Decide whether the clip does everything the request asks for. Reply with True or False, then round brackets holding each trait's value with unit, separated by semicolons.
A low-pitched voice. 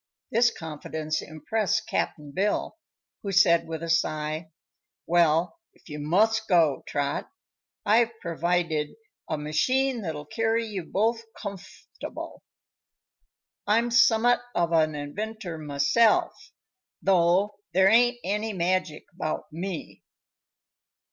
False (175 Hz)